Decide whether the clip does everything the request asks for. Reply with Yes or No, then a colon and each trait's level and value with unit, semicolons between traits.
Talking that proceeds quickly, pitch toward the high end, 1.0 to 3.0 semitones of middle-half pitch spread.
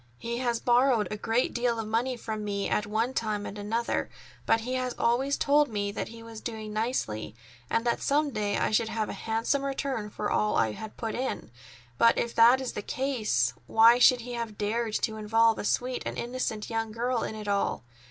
Yes: fast, 210 wpm; high, 230 Hz; narrow, 2.5 semitones